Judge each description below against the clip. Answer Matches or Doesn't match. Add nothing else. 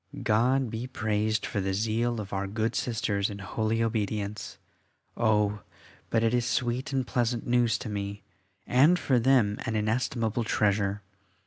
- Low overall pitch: Matches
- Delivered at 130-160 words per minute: Matches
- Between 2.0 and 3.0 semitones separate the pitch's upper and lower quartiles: Matches